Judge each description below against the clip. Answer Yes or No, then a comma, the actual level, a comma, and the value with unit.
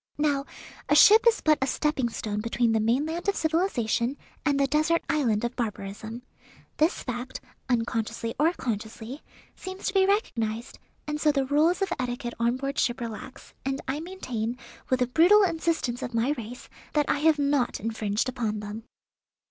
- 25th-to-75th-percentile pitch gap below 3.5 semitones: No, average, 4.9 semitones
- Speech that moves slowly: No, average, 170 wpm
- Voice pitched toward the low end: No, very high, 260 Hz